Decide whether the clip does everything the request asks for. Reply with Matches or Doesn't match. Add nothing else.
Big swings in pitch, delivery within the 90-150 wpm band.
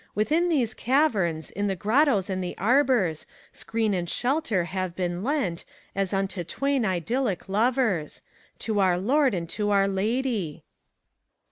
Matches